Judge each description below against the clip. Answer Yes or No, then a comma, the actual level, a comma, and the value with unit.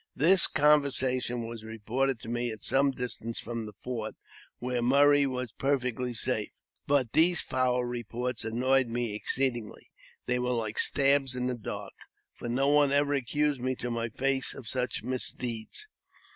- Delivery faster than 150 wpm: Yes, average, 160 wpm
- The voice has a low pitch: Yes, low, 125 Hz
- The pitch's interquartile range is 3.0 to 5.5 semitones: No, narrow, 2.5 semitones